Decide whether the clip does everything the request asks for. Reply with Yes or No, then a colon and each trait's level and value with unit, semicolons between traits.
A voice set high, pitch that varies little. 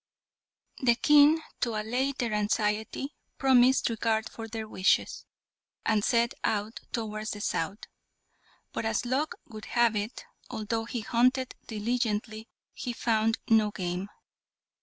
Yes: high, 225 Hz; narrow, 2.3 semitones